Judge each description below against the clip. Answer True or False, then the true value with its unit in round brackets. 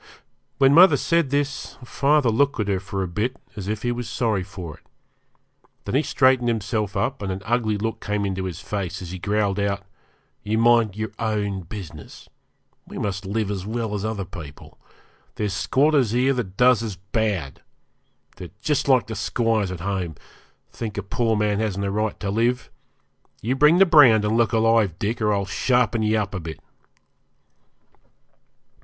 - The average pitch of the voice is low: True (110 Hz)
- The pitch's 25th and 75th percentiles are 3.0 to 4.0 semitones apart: True (3.4 semitones)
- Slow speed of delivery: False (180 wpm)